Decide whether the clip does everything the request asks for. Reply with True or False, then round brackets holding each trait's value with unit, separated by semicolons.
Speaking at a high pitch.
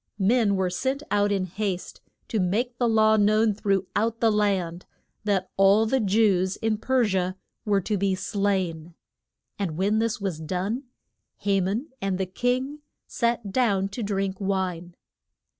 True (200 Hz)